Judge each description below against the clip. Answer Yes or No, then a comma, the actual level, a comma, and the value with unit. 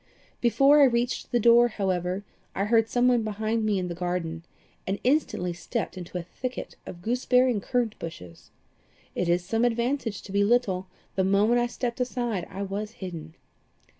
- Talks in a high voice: Yes, high, 215 Hz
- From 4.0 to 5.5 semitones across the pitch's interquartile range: Yes, average, 4.9 semitones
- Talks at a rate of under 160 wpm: No, average, 180 wpm